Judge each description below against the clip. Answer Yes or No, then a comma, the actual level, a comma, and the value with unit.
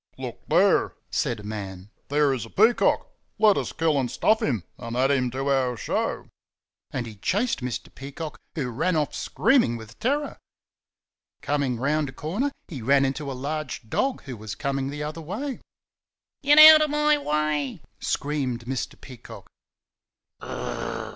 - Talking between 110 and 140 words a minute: No, average, 160 wpm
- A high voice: No, medium, 140 Hz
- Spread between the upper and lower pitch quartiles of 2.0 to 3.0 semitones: No, average, 4.9 semitones